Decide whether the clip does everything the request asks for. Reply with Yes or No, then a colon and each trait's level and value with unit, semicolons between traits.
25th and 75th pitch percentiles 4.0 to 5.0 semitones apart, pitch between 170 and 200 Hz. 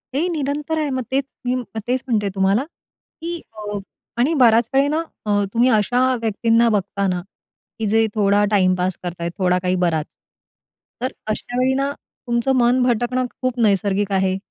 No: average, 4.5 semitones; high, 230 Hz